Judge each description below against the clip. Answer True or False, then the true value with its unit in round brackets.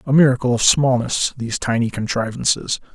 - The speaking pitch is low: True (125 Hz)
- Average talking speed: True (145 wpm)